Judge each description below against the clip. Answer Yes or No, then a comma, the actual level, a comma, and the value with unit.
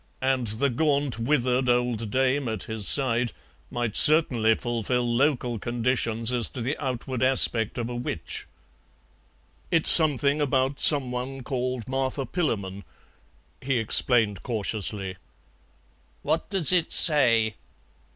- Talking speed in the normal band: No, slow, 120 wpm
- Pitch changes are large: No, average, 2.8 semitones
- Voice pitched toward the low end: Yes, low, 125 Hz